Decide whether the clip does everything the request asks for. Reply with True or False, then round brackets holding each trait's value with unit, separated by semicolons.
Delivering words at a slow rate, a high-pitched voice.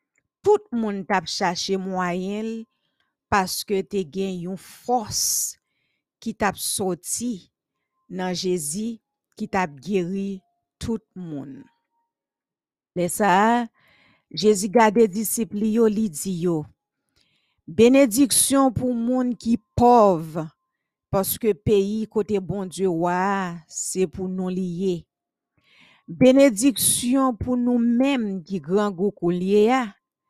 True (95 wpm; 205 Hz)